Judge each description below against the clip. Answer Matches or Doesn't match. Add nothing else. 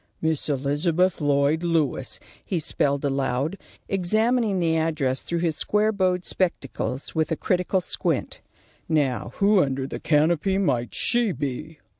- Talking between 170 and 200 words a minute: Doesn't match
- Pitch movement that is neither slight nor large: Matches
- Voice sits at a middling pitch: Matches